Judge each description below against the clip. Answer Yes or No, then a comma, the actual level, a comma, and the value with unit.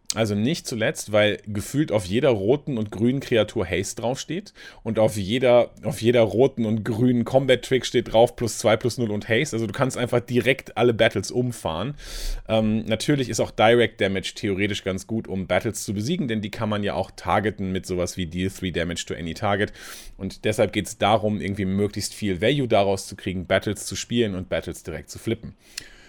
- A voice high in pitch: No, low, 110 Hz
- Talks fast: Yes, fast, 200 wpm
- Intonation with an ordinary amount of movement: Yes, average, 3.3 semitones